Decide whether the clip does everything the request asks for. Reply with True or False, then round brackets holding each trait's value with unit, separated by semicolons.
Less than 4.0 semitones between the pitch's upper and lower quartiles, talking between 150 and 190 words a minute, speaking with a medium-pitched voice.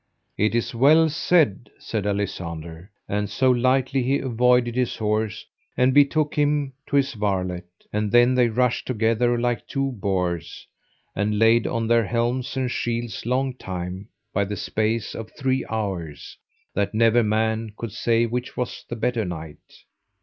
False (3.5 semitones; 155 wpm; 115 Hz)